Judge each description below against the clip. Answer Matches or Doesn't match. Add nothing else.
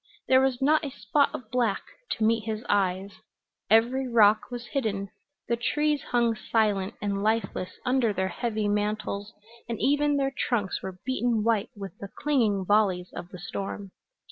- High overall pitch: Matches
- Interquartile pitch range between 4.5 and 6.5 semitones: Doesn't match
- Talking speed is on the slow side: Doesn't match